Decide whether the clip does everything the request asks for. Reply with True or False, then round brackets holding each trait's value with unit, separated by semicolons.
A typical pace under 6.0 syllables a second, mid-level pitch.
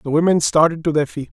False (6.5 syllables/s; 155 Hz)